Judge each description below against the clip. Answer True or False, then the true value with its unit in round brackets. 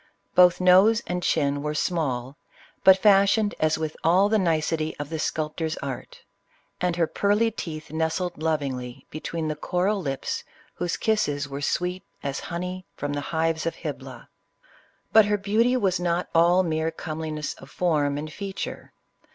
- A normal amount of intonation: True (3.4 semitones)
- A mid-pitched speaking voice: True (165 Hz)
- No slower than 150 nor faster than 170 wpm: True (155 wpm)